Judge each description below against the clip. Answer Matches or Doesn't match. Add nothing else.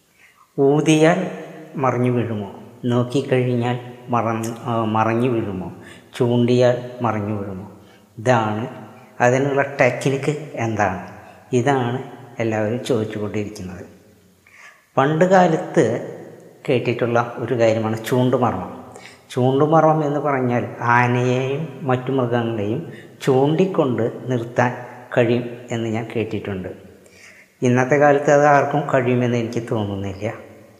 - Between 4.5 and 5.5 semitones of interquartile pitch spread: Doesn't match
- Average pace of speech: Matches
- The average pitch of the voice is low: Matches